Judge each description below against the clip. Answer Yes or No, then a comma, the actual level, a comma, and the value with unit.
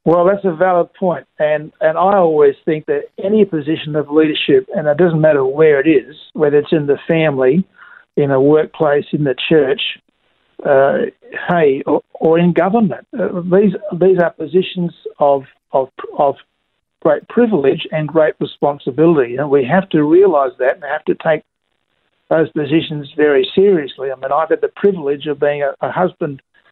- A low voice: No, medium, 165 Hz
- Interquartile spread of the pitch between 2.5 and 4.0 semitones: No, average, 4.7 semitones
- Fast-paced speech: No, average, 175 wpm